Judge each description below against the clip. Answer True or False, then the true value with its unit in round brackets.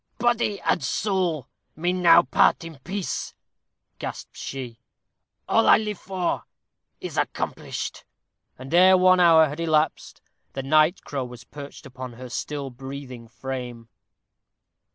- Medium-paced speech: False (130 wpm)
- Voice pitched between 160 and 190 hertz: False (150 Hz)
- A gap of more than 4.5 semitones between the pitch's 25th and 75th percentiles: True (5.6 semitones)